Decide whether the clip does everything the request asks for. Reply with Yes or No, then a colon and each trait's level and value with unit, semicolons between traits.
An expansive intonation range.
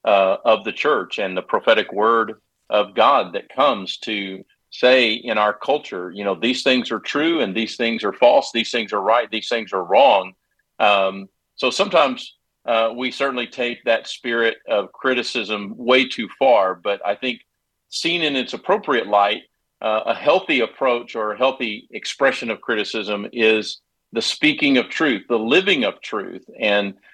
No: average, 3.3 semitones